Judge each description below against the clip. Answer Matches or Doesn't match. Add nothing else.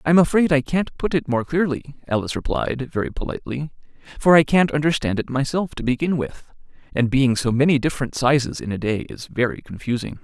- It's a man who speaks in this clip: Matches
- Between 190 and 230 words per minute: Matches